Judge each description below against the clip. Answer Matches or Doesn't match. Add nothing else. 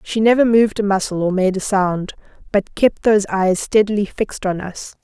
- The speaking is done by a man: Doesn't match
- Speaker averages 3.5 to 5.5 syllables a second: Matches